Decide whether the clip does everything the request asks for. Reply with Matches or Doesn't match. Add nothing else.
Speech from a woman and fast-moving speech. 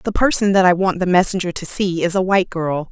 Matches